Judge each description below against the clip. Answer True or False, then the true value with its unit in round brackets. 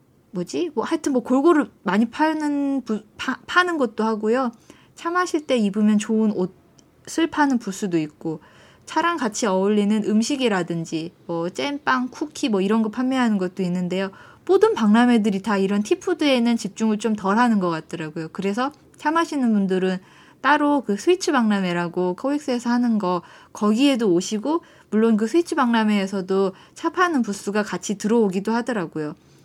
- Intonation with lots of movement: True (6.3 semitones)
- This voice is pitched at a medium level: False (220 Hz)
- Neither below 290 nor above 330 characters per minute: False (340 characters per minute)